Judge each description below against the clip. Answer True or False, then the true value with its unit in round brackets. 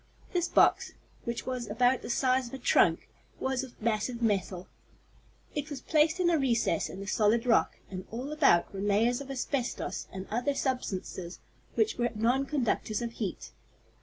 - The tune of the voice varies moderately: True (4.1 semitones)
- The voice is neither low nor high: False (240 Hz)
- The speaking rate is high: False (165 wpm)